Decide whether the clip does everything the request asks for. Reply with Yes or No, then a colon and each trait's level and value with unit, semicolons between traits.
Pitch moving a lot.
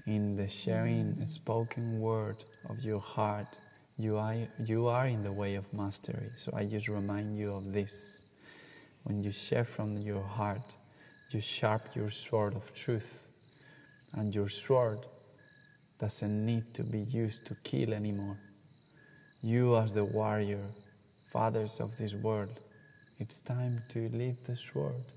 No: average, 3.2 semitones